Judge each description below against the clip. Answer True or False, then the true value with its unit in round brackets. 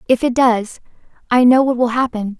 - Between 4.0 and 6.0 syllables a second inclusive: True (5.3 syllables/s)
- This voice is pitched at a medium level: False (240 Hz)